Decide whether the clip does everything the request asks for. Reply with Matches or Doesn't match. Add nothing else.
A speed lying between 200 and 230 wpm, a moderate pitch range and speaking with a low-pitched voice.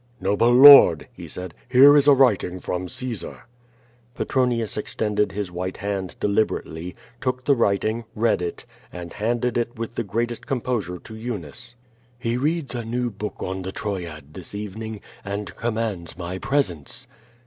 Doesn't match